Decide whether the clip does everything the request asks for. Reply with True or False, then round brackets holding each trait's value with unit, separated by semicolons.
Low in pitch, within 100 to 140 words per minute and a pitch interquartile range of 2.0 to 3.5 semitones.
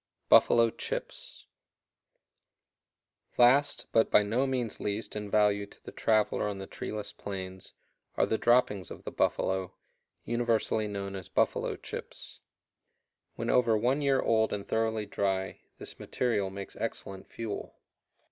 True (105 Hz; 135 wpm; 2.8 semitones)